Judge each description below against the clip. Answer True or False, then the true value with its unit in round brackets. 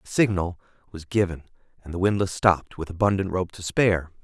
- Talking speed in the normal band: True (185 wpm)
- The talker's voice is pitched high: False (90 Hz)